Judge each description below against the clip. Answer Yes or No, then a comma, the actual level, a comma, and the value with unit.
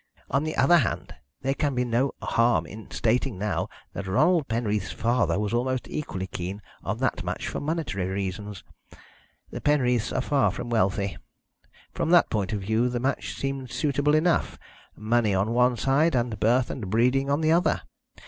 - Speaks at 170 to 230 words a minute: Yes, average, 175 wpm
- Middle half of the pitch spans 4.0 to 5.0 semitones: Yes, average, 4.7 semitones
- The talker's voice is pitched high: No, low, 120 Hz